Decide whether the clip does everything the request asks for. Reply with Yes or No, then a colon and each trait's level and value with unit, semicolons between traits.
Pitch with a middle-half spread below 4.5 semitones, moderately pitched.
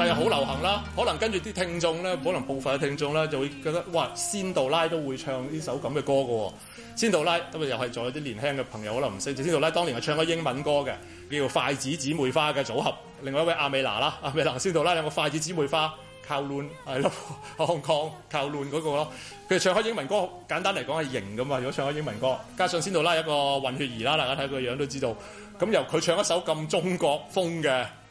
Yes: average, 3.4 semitones; medium, 145 Hz